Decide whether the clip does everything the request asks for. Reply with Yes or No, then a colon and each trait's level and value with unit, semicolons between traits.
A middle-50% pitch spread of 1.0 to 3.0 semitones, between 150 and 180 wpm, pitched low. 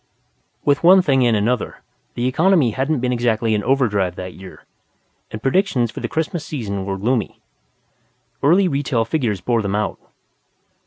No: average, 5.2 semitones; average, 155 wpm; low, 120 Hz